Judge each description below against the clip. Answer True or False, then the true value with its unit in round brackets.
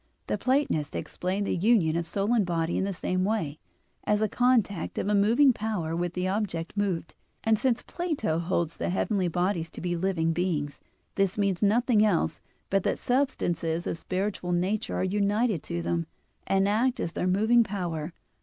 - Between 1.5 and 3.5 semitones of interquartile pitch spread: False (4.0 semitones)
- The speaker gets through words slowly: False (180 wpm)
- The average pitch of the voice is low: False (190 Hz)